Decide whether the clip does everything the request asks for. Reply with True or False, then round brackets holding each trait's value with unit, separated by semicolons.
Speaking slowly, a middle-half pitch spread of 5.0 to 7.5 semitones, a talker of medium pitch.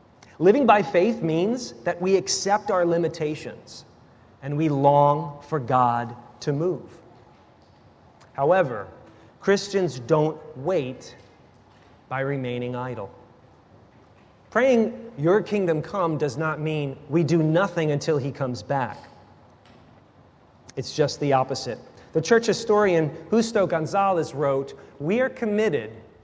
True (115 wpm; 5.6 semitones; 155 Hz)